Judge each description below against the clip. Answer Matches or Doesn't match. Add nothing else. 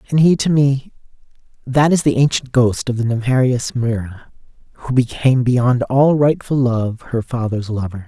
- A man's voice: Matches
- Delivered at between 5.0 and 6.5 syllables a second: Doesn't match